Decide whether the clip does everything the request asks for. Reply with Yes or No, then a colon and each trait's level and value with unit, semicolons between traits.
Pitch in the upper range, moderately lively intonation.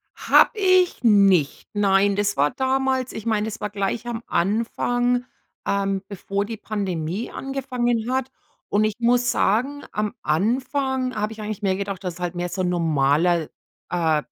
Yes: high, 210 Hz; average, 4.5 semitones